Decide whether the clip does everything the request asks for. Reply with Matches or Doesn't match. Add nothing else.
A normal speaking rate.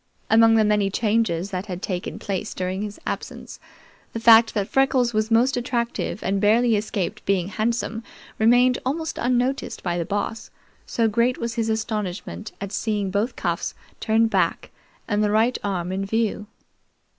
Matches